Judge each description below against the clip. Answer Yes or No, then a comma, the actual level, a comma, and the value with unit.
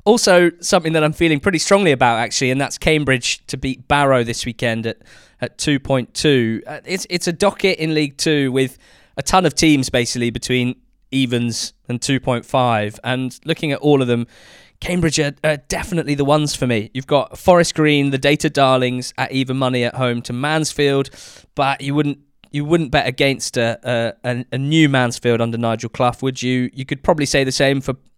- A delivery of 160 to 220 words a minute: Yes, average, 190 wpm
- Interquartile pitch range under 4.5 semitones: Yes, average, 3.5 semitones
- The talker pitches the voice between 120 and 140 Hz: Yes, low, 135 Hz